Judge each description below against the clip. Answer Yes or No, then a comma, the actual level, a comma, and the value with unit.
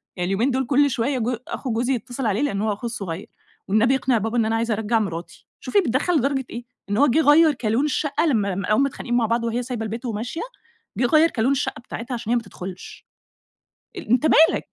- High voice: Yes, high, 240 Hz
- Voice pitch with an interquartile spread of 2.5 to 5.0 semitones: Yes, average, 3.5 semitones